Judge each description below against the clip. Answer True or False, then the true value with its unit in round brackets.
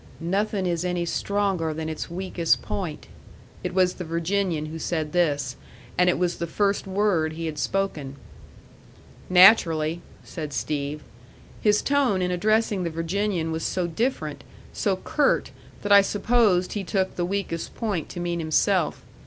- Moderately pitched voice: True (180 Hz)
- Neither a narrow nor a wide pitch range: True (3.5 semitones)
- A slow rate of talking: False (155 wpm)